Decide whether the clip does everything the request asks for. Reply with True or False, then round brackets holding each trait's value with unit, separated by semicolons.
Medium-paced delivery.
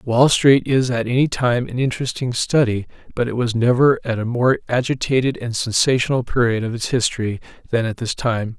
True (190 wpm)